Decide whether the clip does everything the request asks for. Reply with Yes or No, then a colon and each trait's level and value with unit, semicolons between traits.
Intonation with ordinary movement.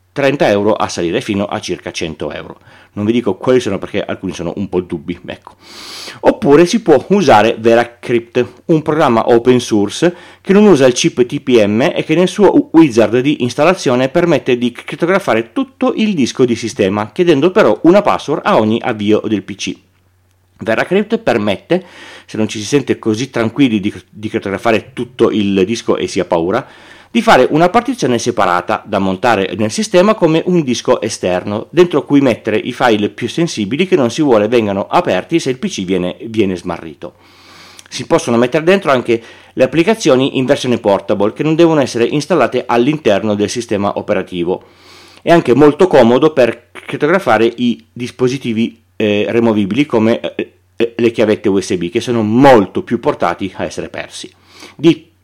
No: wide, 6.5 semitones